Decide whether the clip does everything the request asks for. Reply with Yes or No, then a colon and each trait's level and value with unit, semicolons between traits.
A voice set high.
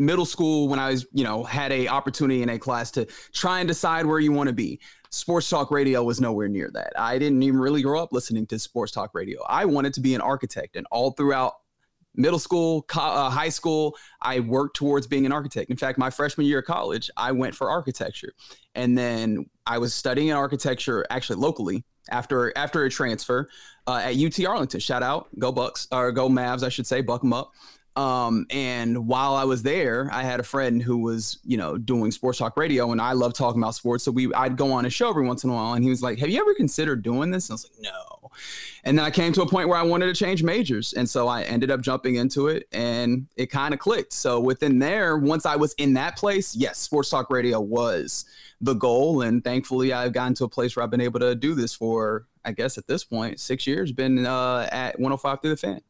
No: low, 130 Hz